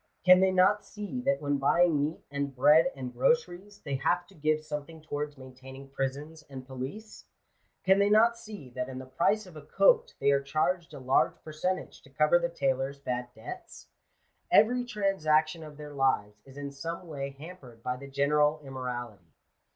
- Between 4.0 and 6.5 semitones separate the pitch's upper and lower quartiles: Yes, average, 5.0 semitones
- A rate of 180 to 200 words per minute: Yes, average, 185 wpm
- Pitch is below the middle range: No, medium, 150 Hz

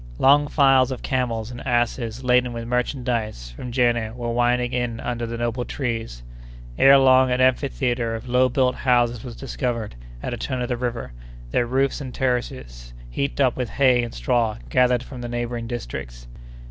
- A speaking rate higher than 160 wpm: Yes, average, 175 wpm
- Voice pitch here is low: Yes, low, 120 Hz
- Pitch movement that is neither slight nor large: No, narrow, 1.6 semitones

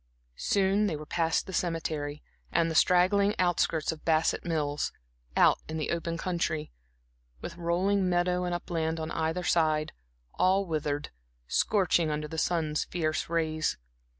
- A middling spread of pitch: No, narrow, 2.3 semitones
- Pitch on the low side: No, medium, 165 Hz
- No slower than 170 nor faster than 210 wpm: No, average, 145 wpm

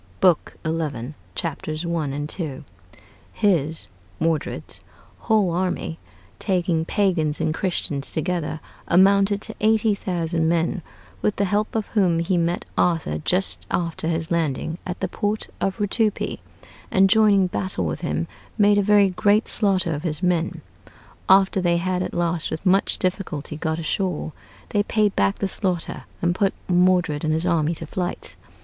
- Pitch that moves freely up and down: No, average, 3.2 semitones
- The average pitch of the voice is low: No, medium, 175 Hz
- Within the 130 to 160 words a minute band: Yes, average, 155 wpm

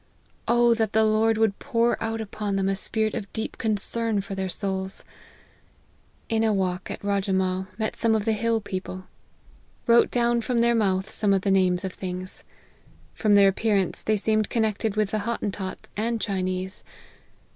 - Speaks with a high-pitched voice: Yes, high, 210 Hz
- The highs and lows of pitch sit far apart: No, narrow, 2.6 semitones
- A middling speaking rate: Yes, average, 170 wpm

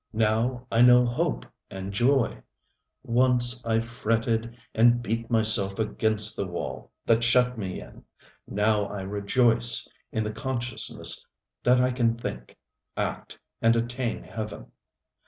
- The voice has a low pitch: Yes, low, 115 Hz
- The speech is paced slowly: Yes, slow, 130 wpm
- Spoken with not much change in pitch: Yes, narrow, 2.2 semitones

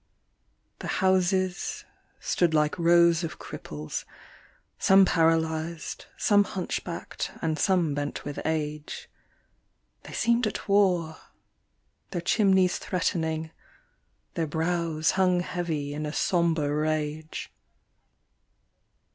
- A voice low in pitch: No, medium, 165 Hz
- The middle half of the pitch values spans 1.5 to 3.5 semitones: Yes, average, 2.8 semitones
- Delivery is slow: Yes, slow, 100 wpm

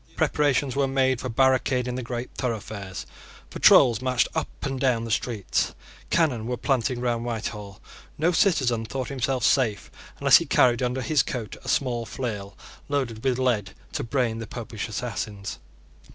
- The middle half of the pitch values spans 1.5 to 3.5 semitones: Yes, narrow, 2.6 semitones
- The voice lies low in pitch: Yes, low, 125 Hz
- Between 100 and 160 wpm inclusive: Yes, average, 155 wpm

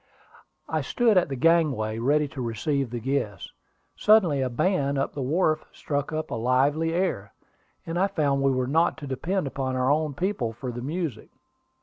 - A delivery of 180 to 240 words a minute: Yes, average, 185 wpm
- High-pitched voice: No, medium, 140 Hz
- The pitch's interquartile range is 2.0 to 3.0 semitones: No, average, 4.2 semitones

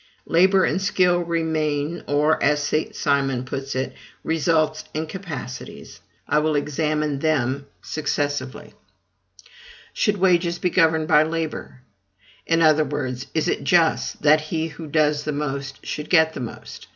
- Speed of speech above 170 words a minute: No, average, 140 wpm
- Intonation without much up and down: Yes, narrow, 2.3 semitones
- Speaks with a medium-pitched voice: Yes, medium, 155 Hz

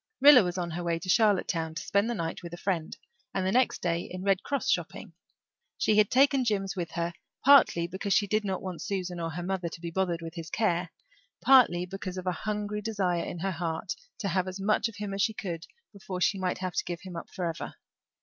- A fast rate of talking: Yes, fast, 235 wpm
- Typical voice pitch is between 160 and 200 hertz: Yes, medium, 185 Hz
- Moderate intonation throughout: Yes, average, 3.0 semitones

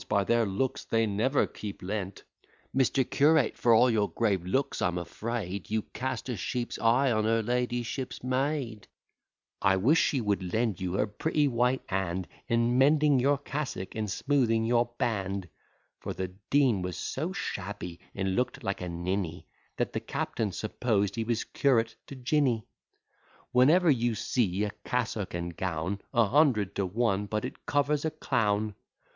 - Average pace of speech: Yes, average, 165 wpm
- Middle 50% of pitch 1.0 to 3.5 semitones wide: No, average, 4.7 semitones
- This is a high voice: No, low, 115 Hz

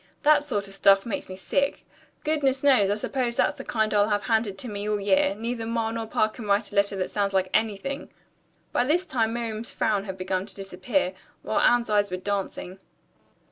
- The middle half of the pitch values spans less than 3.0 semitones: No, average, 3.4 semitones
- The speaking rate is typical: No, fast, 210 wpm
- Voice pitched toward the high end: Yes, high, 215 Hz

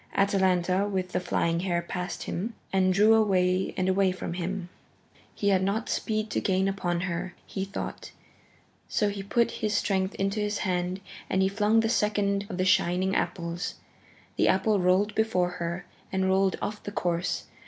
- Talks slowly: No, average, 175 wpm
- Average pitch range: No, narrow, 2.0 semitones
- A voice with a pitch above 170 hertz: Yes, high, 190 Hz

